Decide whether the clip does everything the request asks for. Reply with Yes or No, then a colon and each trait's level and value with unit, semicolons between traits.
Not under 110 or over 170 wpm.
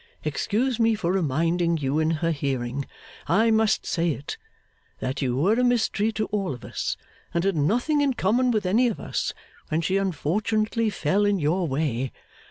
No: average, 180 wpm